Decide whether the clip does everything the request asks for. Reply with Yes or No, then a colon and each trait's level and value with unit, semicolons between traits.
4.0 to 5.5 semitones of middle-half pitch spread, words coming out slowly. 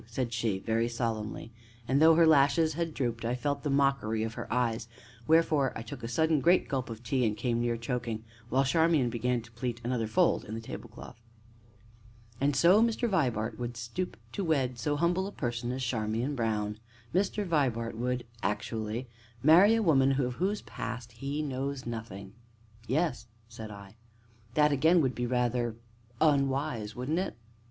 No: average, 4.3 semitones; average, 175 wpm